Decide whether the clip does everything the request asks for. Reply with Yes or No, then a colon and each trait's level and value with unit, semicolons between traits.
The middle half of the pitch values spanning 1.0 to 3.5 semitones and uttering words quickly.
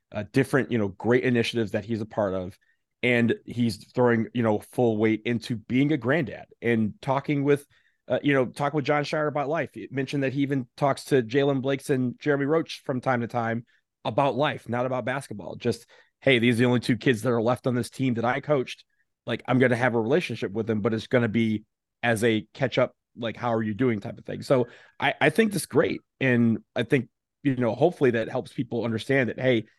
Yes: average, 3.0 semitones; fast, 235 wpm